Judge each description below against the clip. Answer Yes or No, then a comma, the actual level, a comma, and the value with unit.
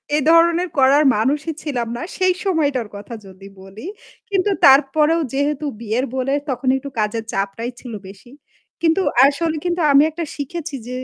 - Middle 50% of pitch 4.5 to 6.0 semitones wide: Yes, wide, 5.6 semitones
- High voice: Yes, very high, 280 Hz